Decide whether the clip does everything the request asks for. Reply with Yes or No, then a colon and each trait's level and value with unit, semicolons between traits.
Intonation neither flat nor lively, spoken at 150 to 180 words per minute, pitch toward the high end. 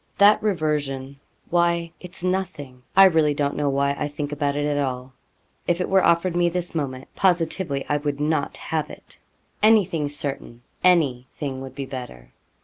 No: average, 3.8 semitones; average, 170 wpm; medium, 150 Hz